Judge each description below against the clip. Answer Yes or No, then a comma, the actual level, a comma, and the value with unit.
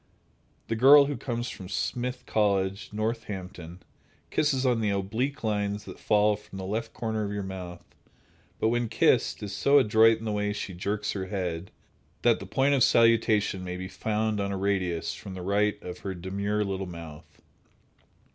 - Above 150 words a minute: Yes, average, 175 wpm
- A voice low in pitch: Yes, low, 105 Hz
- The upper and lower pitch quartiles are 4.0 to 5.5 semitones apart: No, average, 3.0 semitones